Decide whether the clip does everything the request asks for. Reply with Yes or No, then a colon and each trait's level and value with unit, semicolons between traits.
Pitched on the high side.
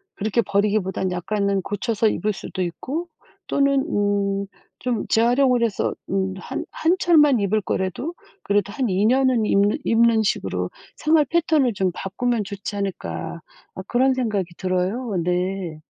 Yes: high, 210 Hz